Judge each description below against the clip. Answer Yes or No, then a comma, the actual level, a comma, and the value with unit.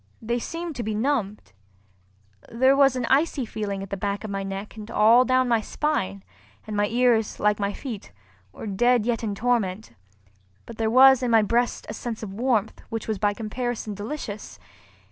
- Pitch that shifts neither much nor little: Yes, average, 3.1 semitones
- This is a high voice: Yes, high, 225 Hz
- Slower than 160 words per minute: No, average, 185 wpm